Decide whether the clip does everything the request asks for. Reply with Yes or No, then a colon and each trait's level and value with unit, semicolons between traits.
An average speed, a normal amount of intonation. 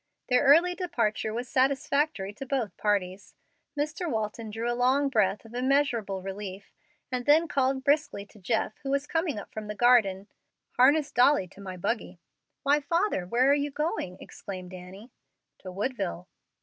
No: average, 160 wpm; wide, 5.9 semitones